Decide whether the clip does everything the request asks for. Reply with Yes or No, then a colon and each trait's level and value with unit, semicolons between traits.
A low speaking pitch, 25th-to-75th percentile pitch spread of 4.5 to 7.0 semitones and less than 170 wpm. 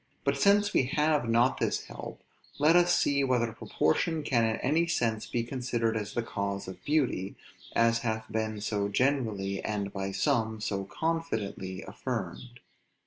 Yes: low, 115 Hz; average, 5.3 semitones; average, 155 wpm